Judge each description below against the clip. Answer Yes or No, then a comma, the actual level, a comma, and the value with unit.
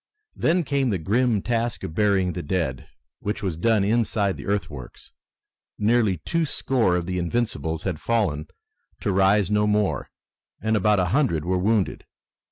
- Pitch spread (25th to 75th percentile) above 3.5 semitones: Yes, average, 4.1 semitones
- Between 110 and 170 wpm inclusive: Yes, average, 160 wpm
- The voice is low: Yes, low, 100 Hz